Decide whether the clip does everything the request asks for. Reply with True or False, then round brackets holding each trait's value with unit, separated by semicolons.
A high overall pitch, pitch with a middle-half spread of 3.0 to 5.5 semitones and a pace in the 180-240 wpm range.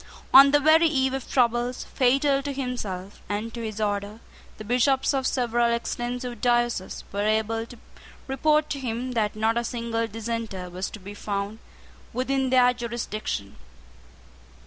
False (235 Hz; 3.3 semitones; 150 wpm)